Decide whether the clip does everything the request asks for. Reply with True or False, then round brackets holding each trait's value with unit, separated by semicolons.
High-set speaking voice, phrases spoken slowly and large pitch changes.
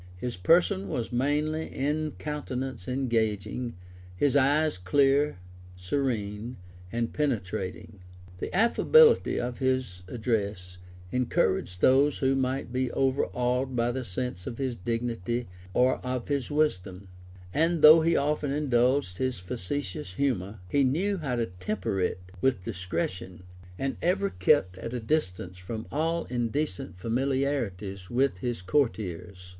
False (125 Hz; 130 wpm; 6.4 semitones)